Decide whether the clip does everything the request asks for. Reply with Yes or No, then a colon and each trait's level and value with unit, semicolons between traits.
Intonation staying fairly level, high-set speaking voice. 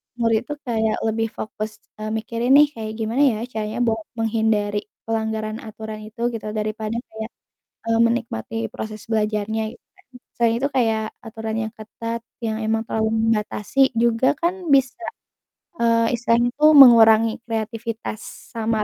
Yes: narrow, 1.2 semitones; high, 225 Hz